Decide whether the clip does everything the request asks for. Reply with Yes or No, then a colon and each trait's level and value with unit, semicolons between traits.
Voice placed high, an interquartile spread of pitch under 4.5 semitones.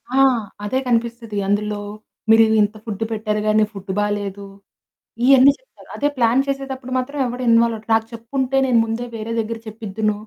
Yes: high, 225 Hz; average, 3.0 semitones